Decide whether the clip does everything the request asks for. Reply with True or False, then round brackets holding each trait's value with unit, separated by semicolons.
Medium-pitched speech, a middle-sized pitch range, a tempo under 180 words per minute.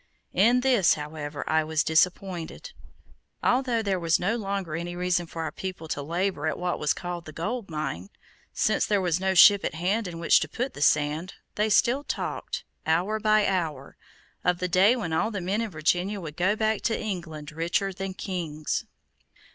False (180 Hz; 4.2 semitones; 185 wpm)